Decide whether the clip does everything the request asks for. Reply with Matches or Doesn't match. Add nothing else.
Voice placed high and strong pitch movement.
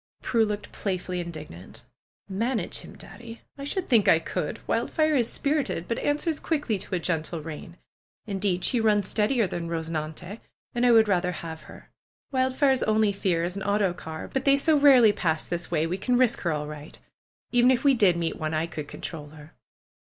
Matches